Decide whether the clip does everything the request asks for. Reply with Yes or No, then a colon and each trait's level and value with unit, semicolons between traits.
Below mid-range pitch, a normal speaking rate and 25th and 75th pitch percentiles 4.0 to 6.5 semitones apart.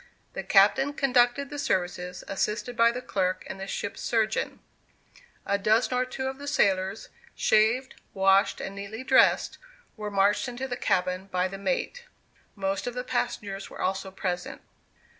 No: high, 210 Hz; average, 160 wpm; average, 4.5 semitones